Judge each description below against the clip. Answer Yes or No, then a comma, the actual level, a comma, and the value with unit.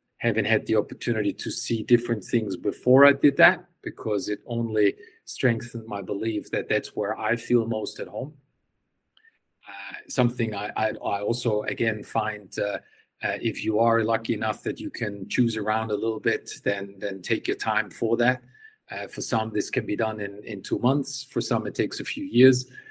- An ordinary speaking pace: Yes, average, 195 wpm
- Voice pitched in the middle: No, low, 115 Hz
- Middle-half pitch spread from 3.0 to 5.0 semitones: No, narrow, 2.6 semitones